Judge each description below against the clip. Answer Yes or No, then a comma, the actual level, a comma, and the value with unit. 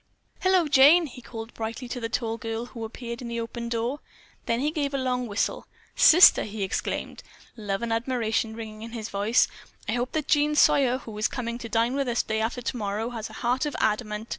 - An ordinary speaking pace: No, fast, 215 wpm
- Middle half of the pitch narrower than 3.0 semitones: Yes, narrow, 2.4 semitones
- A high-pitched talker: Yes, high, 235 Hz